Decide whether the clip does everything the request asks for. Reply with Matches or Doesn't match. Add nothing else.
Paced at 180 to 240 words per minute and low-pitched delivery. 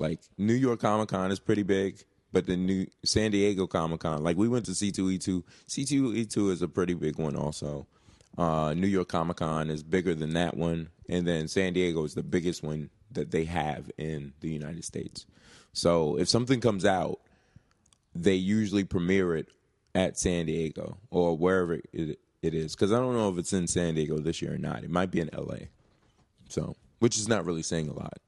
Matches